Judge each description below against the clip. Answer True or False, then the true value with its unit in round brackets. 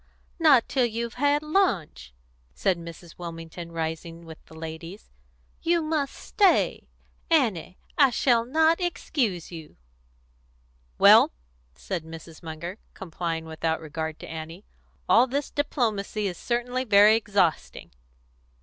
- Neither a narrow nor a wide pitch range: False (7.8 semitones)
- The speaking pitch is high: True (195 Hz)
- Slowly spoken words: True (120 wpm)